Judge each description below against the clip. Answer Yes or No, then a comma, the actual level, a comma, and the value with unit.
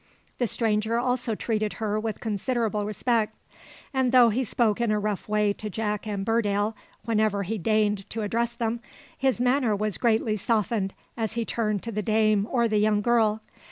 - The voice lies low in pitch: No, high, 220 Hz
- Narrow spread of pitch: Yes, narrow, 1.8 semitones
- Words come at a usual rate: Yes, average, 180 wpm